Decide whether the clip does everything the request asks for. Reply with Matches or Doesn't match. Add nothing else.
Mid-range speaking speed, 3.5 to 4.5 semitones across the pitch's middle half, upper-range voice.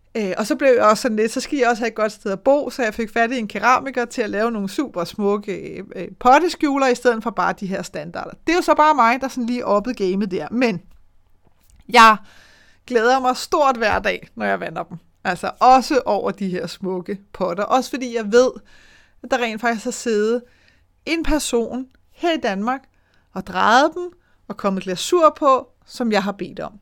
Matches